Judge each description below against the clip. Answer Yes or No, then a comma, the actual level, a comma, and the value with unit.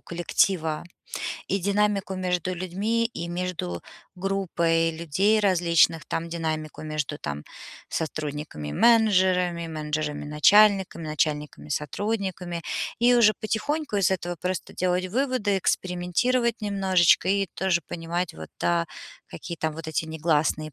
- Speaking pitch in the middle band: Yes, medium, 175 Hz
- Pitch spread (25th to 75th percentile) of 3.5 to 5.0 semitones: Yes, average, 3.9 semitones